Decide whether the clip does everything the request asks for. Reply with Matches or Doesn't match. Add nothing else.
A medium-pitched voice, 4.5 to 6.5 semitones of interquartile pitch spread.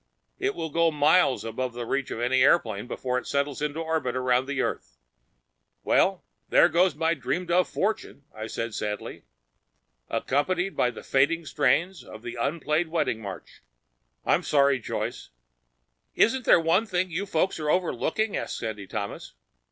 Matches